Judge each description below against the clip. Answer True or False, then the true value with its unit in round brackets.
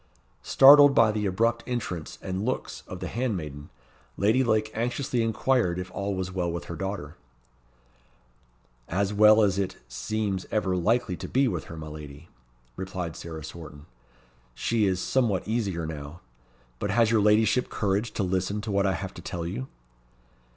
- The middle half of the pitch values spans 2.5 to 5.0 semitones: True (4.4 semitones)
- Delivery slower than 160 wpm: False (165 wpm)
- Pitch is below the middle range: True (100 Hz)